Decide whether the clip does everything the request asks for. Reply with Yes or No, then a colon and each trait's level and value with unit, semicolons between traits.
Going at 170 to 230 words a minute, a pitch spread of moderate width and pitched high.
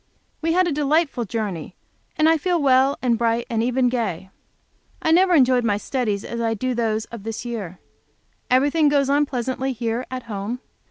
Yes: average, 180 wpm; average, 4.0 semitones; very high, 250 Hz